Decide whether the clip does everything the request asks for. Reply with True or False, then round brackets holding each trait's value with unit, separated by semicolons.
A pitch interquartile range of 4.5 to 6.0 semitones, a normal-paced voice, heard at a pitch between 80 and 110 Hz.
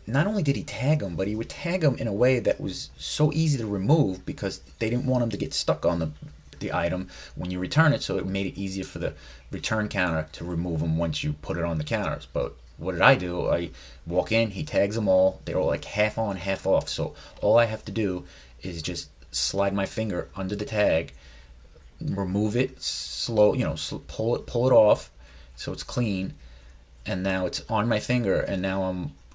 False (5.2 semitones; 225 wpm; 95 Hz)